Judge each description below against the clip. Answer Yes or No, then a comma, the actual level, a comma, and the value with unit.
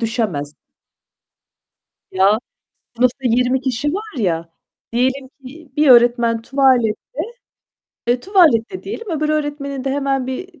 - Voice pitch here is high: Yes, very high, 260 Hz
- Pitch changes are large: No, average, 3.9 semitones